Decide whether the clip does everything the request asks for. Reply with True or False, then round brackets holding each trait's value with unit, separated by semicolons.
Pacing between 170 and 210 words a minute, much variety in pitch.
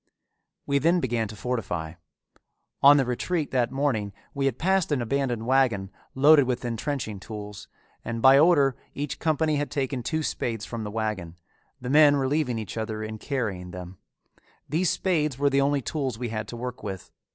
False (175 wpm; 4.6 semitones)